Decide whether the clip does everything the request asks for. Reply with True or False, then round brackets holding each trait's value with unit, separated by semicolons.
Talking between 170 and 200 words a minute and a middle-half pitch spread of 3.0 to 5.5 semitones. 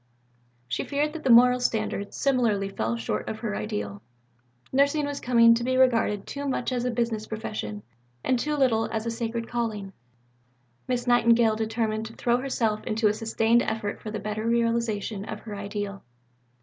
False (175 wpm; 2.6 semitones)